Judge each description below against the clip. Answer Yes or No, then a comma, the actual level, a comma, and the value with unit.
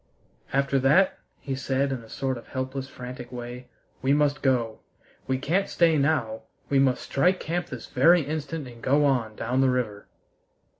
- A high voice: No, low, 135 Hz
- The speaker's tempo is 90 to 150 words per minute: No, average, 170 wpm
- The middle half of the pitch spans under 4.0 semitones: Yes, narrow, 2.6 semitones